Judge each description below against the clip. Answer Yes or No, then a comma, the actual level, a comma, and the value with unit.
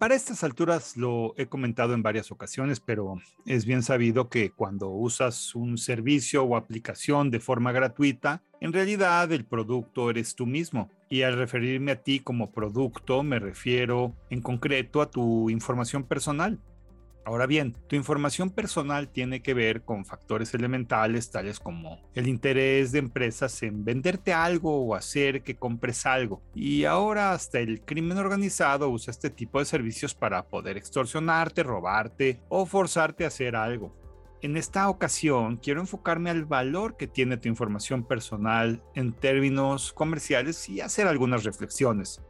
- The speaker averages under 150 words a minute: No, average, 155 wpm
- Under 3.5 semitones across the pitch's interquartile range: No, average, 4.1 semitones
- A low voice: Yes, low, 130 Hz